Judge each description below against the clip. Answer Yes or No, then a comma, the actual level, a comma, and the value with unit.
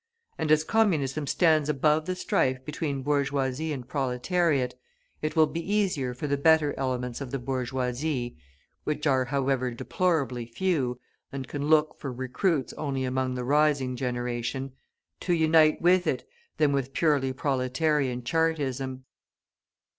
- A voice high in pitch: No, medium, 140 Hz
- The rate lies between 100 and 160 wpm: Yes, average, 140 wpm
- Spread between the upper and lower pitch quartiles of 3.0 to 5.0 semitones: Yes, average, 3.3 semitones